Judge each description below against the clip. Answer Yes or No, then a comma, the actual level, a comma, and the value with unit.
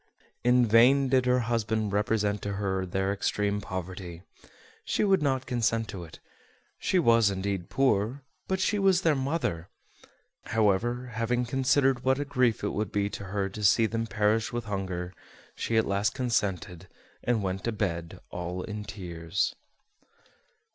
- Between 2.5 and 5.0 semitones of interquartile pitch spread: Yes, average, 4.3 semitones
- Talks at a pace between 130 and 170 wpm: Yes, average, 155 wpm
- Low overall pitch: Yes, low, 110 Hz